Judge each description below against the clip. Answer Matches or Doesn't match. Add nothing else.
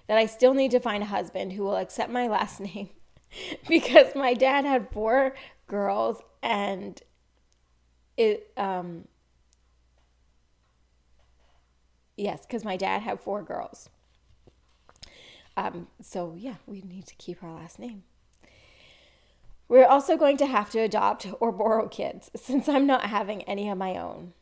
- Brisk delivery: Doesn't match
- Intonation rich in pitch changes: Matches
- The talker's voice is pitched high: Matches